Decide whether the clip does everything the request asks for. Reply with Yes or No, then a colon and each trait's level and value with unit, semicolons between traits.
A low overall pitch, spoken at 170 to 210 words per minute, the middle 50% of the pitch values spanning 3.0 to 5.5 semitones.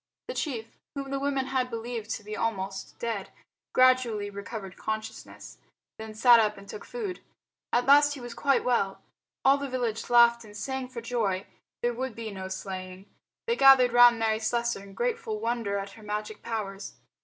No: high, 230 Hz; average, 180 wpm; average, 3.6 semitones